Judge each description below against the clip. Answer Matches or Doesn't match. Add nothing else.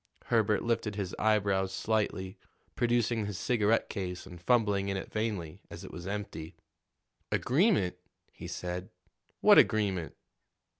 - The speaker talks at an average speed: Doesn't match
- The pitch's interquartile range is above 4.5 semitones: Doesn't match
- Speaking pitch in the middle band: Doesn't match